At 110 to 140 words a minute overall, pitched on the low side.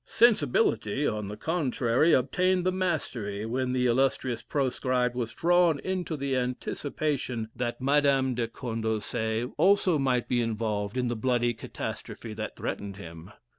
Yes: slow, 135 wpm; low, 125 Hz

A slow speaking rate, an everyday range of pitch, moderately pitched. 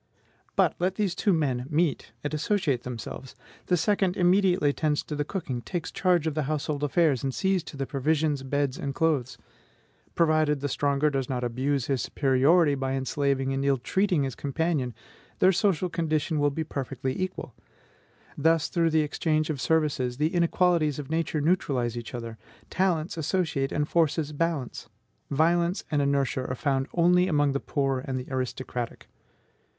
No: average, 165 wpm; average, 3.7 semitones; medium, 150 Hz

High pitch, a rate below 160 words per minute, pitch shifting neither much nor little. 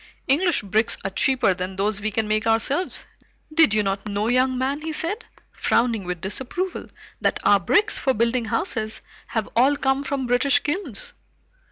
No: high, 240 Hz; average, 170 wpm; average, 4.9 semitones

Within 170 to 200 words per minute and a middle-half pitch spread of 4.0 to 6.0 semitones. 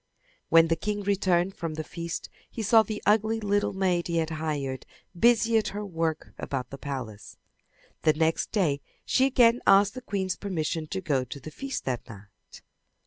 Yes: average, 180 wpm; average, 5.0 semitones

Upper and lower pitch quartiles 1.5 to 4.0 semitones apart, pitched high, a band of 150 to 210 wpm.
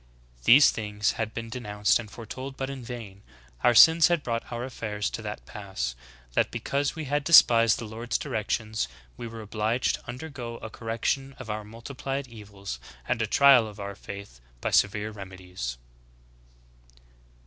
No: average, 3.5 semitones; low, 115 Hz; average, 165 wpm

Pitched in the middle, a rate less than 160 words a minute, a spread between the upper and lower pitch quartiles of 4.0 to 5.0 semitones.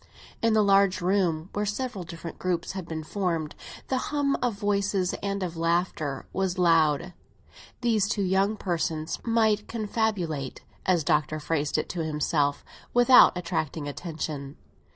Yes: medium, 180 Hz; average, 150 wpm; average, 4.3 semitones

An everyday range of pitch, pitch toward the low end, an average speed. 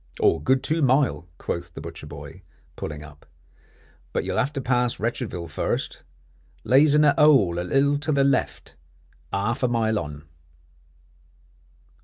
No: wide, 8.3 semitones; low, 120 Hz; average, 145 wpm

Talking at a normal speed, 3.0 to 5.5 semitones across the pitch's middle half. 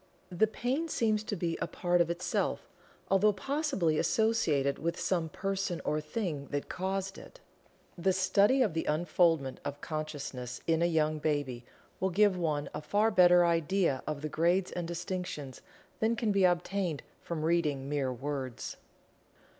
Yes: average, 155 wpm; average, 4.3 semitones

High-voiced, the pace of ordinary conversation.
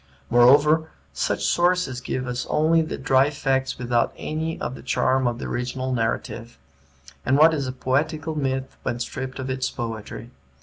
No: low, 130 Hz; average, 165 wpm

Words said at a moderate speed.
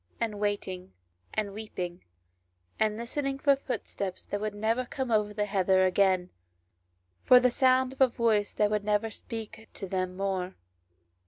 Yes: average, 165 wpm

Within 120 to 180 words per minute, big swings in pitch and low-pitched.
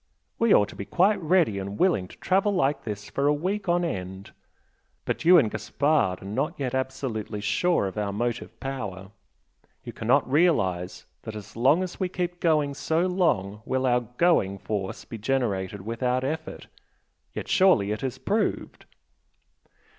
Yes: average, 165 wpm; wide, 8.8 semitones; low, 130 Hz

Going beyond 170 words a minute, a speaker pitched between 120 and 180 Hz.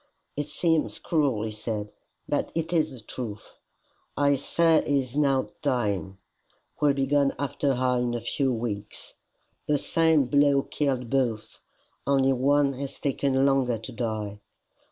No: average, 150 wpm; low, 135 Hz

